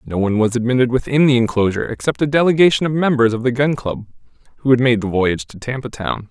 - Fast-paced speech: Yes, fast, 230 wpm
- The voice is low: Yes, low, 125 Hz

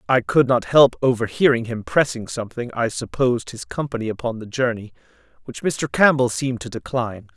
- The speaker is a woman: No, male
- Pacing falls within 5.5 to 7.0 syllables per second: Yes, 5.6 syllables/s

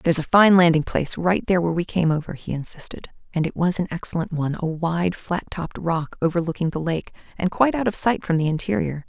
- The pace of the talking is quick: Yes, fast, 225 wpm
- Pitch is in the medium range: Yes, medium, 170 Hz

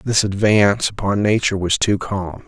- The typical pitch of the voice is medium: No, low, 100 Hz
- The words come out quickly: No, average, 170 wpm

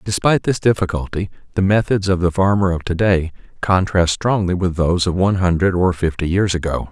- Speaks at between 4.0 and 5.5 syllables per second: No, 5.8 syllables/s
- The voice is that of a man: Yes, male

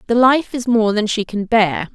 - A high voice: Yes, high, 225 Hz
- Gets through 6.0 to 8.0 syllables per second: No, 4.6 syllables/s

